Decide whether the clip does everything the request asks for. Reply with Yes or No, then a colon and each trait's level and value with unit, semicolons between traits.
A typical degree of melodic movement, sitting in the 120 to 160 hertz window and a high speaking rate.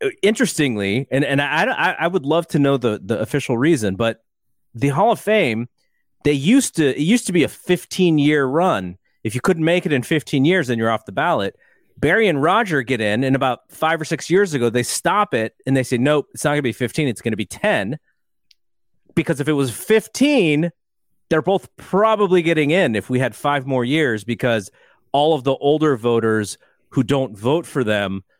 No: wide, 5.7 semitones; medium, 140 Hz; fast, 210 wpm